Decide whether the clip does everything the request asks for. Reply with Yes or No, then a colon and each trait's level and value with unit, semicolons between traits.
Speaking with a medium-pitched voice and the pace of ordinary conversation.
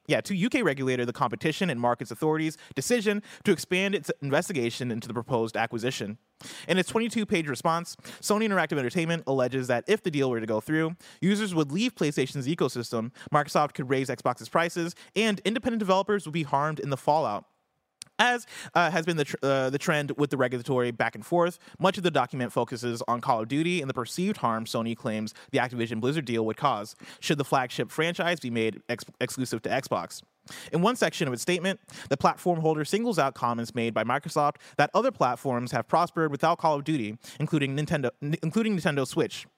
Yes: medium, 150 Hz; average, 195 wpm